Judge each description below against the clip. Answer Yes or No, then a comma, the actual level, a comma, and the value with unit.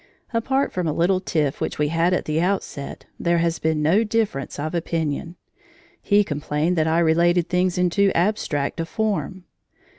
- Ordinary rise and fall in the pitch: Yes, average, 3.0 semitones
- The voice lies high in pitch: No, medium, 170 Hz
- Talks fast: No, average, 175 wpm